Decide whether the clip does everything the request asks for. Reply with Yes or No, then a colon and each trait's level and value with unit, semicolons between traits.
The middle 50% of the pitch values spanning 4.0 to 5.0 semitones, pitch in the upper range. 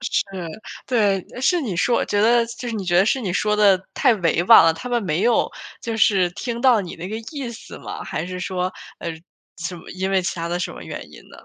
Yes: average, 4.6 semitones; high, 205 Hz